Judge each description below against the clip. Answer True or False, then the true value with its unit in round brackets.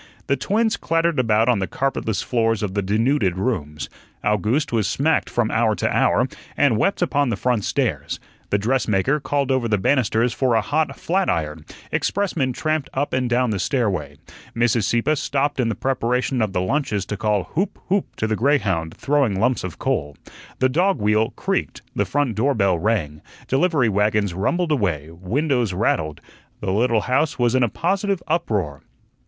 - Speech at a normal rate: True (175 wpm)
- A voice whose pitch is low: True (115 Hz)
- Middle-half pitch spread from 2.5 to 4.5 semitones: False (5.6 semitones)